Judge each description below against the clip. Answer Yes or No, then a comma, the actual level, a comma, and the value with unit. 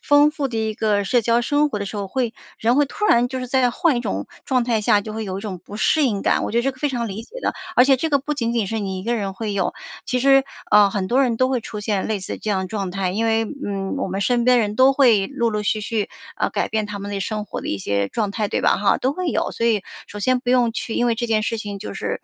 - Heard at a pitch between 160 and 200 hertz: No, high, 225 Hz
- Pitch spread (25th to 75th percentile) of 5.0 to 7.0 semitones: No, average, 3.8 semitones